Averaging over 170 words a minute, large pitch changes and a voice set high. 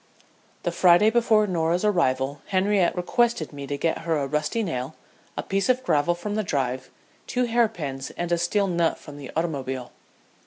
No: average, 180 wpm; wide, 6.3 semitones; medium, 170 Hz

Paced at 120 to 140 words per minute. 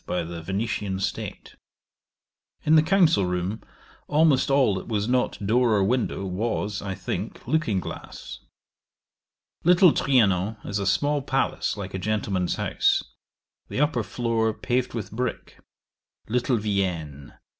Yes: slow, 135 wpm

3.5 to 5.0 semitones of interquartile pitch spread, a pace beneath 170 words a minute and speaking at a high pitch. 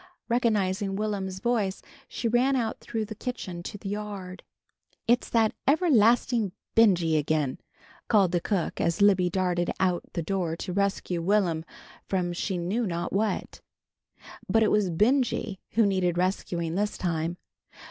Yes: average, 3.8 semitones; average, 145 wpm; high, 195 Hz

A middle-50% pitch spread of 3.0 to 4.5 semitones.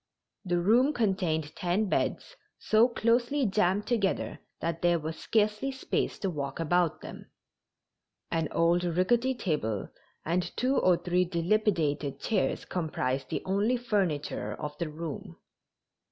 No: average, 4.9 semitones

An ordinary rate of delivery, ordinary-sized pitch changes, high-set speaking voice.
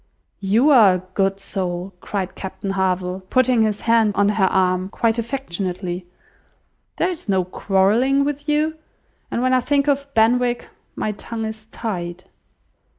Yes: average, 150 wpm; average, 4.7 semitones; high, 210 Hz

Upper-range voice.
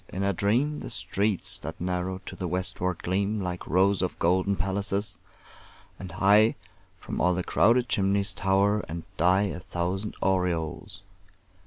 No: very low, 95 Hz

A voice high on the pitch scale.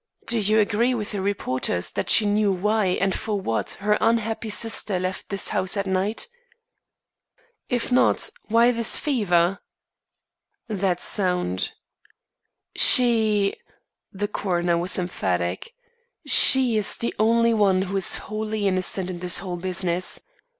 Yes: high, 200 Hz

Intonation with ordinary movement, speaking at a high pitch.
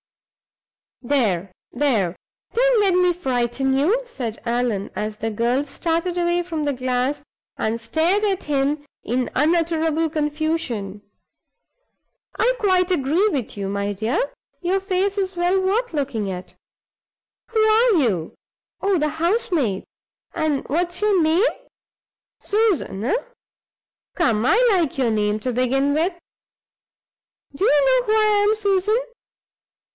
No: wide, 7.6 semitones; very high, 315 Hz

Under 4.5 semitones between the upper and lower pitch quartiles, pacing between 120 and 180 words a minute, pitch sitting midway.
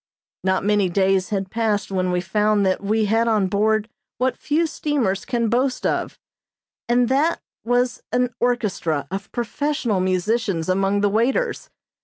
No: average, 4.0 semitones; average, 150 wpm; high, 215 Hz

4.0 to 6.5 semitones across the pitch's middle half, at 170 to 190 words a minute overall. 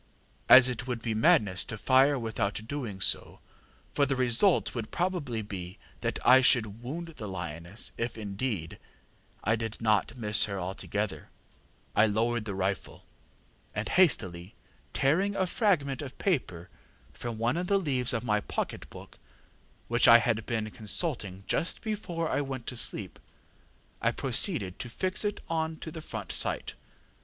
No: average, 5.3 semitones; average, 155 wpm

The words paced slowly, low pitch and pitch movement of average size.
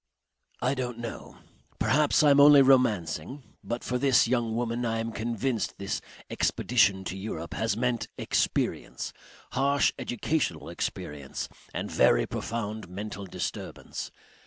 Yes: slow, 130 wpm; low, 115 Hz; average, 3.9 semitones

